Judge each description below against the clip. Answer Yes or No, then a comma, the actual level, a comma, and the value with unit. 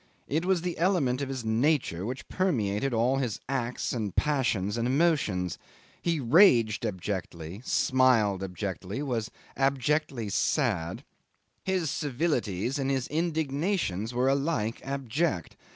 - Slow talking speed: Yes, slow, 120 wpm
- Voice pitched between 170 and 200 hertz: No, low, 130 Hz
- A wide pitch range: Yes, wide, 5.8 semitones